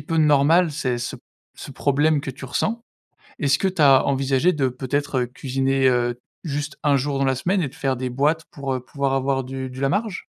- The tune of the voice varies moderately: No, narrow, 2.1 semitones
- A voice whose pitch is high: No, medium, 140 Hz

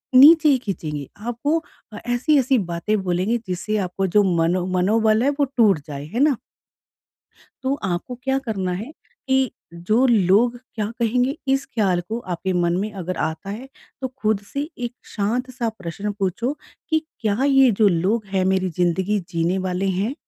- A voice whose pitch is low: No, high, 215 Hz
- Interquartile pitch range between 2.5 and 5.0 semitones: No, wide, 5.4 semitones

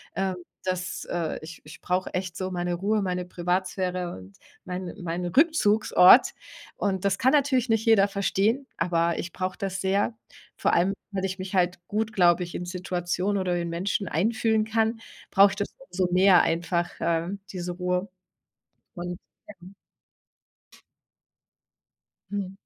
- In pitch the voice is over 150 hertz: Yes, medium, 185 Hz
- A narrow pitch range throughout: Yes, narrow, 2.2 semitones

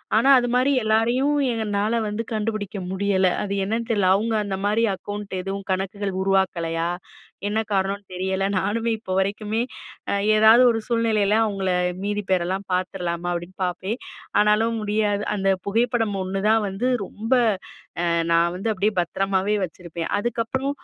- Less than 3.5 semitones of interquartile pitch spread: Yes, average, 2.7 semitones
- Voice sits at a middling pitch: No, high, 205 Hz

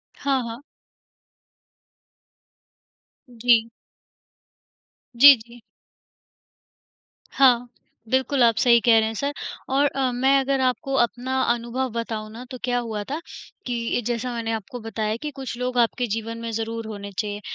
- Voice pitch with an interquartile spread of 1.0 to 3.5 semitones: Yes, narrow, 2.4 semitones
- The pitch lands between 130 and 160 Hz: No, high, 240 Hz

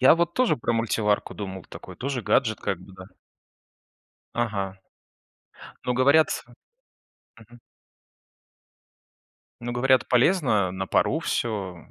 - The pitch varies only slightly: No, average, 4.8 semitones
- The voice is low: Yes, low, 115 Hz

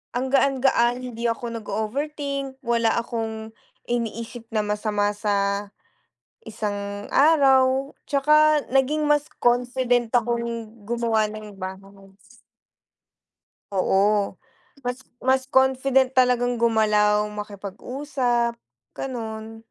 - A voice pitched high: Yes, high, 235 Hz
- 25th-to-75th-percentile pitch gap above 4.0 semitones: No, average, 3.7 semitones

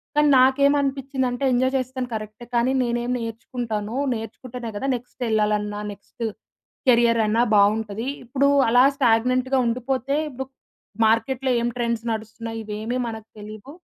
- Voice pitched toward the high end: Yes, high, 235 Hz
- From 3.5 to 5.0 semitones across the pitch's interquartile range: No, average, 2.7 semitones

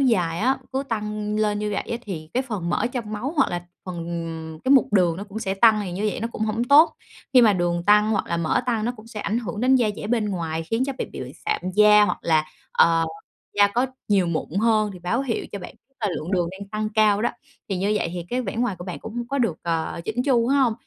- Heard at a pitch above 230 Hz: No, high, 210 Hz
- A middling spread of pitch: Yes, average, 4.4 semitones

